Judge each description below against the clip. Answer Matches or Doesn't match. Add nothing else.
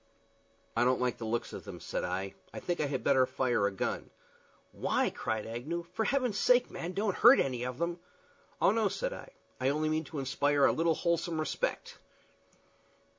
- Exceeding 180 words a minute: Matches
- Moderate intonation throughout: Doesn't match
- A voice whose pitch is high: Doesn't match